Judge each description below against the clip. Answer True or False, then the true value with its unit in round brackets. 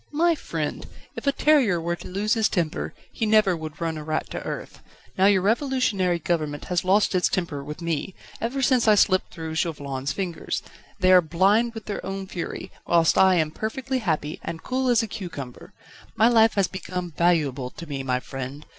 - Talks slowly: False (195 wpm)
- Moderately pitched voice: True (180 Hz)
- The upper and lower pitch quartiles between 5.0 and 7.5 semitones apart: True (5.5 semitones)